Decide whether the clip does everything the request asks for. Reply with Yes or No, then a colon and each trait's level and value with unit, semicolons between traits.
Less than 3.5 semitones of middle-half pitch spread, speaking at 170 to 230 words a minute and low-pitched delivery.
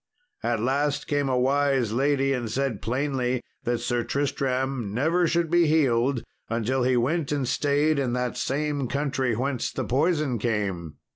No: average, 2.9 semitones; average, 155 wpm; low, 130 Hz